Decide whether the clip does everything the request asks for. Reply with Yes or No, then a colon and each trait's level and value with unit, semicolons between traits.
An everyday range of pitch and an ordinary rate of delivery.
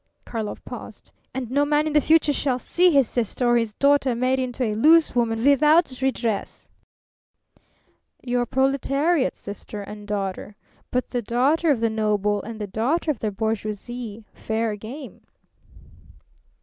Yes: average, 4.4 semitones; average, 150 wpm